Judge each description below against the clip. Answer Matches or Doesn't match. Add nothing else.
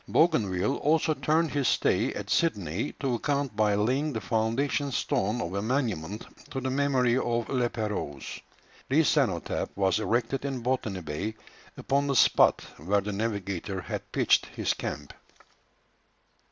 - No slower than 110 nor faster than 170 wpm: Matches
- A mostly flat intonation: Doesn't match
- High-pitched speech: Doesn't match